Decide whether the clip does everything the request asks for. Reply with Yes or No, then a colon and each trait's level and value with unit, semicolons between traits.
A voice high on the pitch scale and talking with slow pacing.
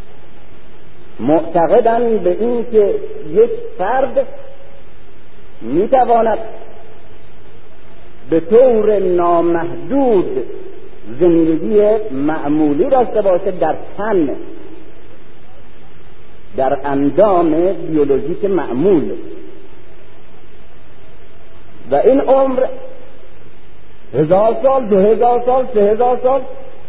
Yes: high, 235 Hz; slow, 70 wpm